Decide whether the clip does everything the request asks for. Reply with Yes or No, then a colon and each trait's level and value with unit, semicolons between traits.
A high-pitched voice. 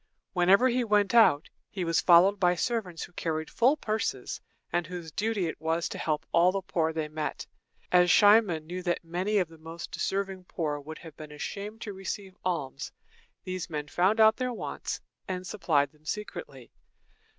No: medium, 180 Hz